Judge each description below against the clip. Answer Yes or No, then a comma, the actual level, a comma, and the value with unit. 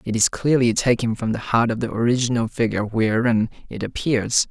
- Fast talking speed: No, average, 185 wpm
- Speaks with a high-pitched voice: No, low, 115 Hz